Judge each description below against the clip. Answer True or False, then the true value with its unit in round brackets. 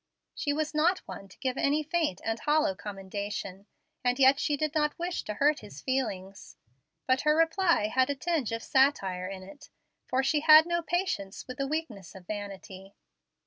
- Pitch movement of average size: False (7.3 semitones)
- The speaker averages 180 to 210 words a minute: True (185 wpm)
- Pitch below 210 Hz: False (265 Hz)